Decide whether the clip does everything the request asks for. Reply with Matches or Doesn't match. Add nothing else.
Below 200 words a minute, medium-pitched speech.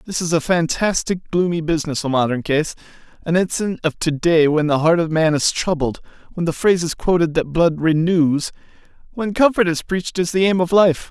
Doesn't match